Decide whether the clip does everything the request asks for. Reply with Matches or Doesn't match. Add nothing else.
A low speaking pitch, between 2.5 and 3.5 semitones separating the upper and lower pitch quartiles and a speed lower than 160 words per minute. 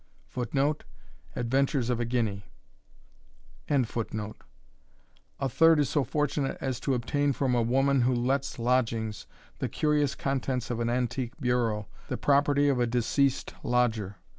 Matches